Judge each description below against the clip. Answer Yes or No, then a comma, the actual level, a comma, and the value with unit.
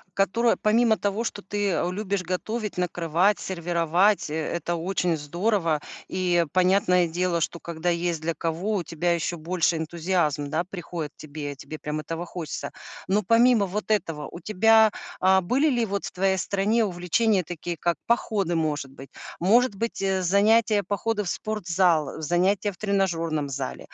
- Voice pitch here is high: No, medium, 180 Hz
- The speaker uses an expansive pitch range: No, average, 3.6 semitones